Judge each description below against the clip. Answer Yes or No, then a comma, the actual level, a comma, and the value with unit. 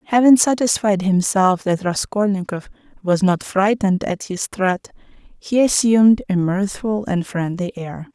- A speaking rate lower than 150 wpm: Yes, slow, 135 wpm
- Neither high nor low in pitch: No, high, 195 Hz